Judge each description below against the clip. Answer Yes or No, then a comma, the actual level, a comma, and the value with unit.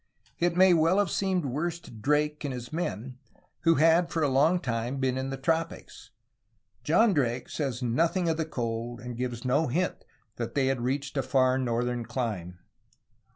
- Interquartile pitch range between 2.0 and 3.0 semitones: No, average, 5.0 semitones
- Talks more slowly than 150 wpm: No, average, 180 wpm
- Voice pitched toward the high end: No, low, 135 Hz